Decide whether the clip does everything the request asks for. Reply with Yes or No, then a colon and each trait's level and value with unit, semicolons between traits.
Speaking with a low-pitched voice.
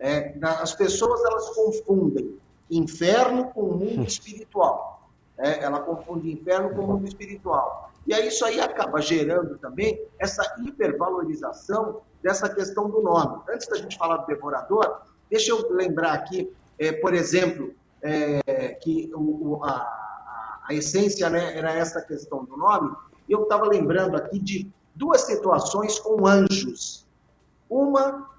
No: high, 195 Hz